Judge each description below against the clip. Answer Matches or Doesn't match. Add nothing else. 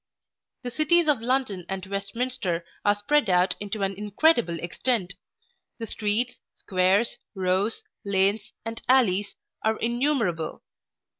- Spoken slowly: Matches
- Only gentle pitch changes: Doesn't match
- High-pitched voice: Matches